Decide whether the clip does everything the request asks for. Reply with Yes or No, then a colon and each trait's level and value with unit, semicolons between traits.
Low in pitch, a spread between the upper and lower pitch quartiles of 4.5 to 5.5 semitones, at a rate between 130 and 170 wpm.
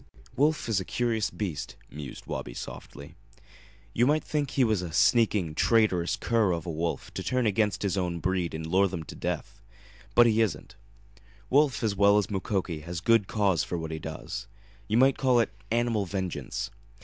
No: low, 100 Hz; average, 5.0 semitones; average, 185 wpm